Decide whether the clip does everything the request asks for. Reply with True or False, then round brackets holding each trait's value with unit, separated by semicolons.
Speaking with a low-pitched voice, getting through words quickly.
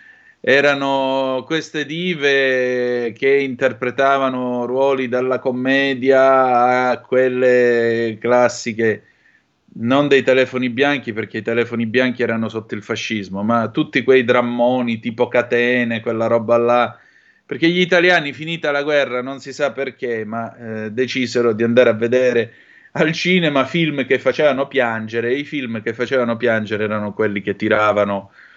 False (125 Hz; 135 wpm)